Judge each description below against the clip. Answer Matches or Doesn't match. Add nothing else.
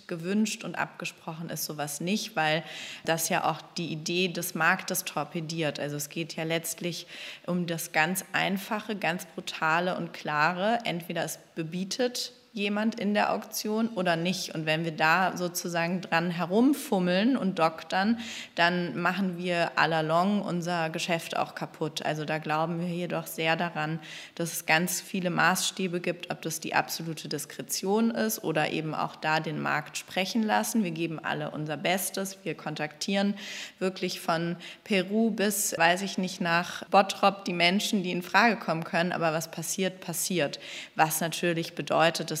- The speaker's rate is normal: Matches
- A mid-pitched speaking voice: Matches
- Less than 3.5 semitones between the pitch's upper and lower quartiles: Matches